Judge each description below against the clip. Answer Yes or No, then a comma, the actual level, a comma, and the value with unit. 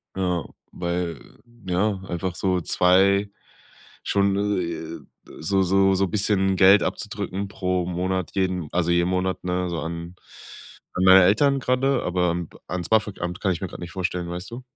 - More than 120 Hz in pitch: No, very low, 90 Hz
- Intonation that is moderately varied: No, narrow, 1.9 semitones